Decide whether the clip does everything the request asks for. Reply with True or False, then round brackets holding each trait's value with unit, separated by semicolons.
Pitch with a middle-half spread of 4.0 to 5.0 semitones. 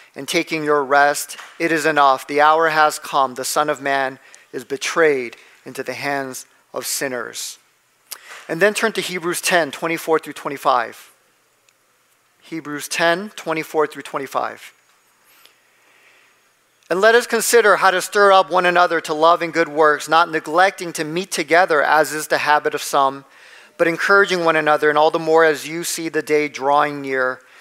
False (3.1 semitones)